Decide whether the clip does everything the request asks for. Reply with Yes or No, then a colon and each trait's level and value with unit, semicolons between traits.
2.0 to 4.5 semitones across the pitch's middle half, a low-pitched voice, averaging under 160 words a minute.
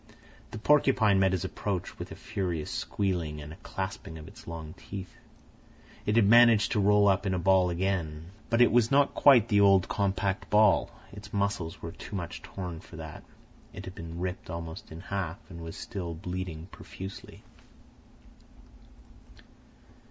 No: average, 3.4 semitones; very low, 95 Hz; average, 165 wpm